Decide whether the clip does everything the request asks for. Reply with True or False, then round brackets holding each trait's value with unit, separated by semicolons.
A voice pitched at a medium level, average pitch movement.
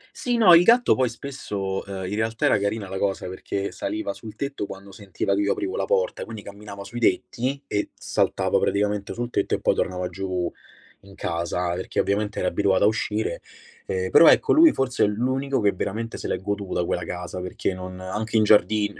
False (105 Hz; 3.8 semitones)